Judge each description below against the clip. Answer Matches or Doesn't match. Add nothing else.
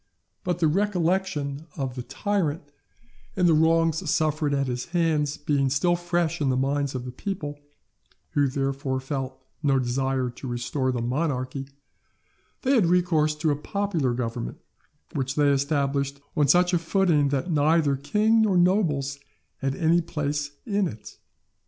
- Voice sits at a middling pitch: Matches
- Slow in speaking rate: Doesn't match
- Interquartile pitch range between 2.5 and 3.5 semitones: Doesn't match